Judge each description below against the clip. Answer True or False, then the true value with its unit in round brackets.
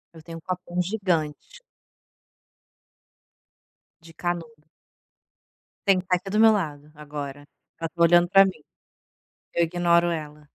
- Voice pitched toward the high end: False (170 Hz)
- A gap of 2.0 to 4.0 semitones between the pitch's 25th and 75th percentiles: True (3.1 semitones)